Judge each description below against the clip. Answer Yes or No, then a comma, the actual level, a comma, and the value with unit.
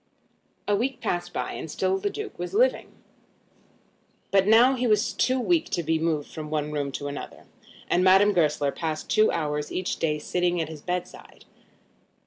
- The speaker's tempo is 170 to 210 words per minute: Yes, average, 175 wpm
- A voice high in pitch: No, medium, 180 Hz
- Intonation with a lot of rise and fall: Yes, wide, 6.7 semitones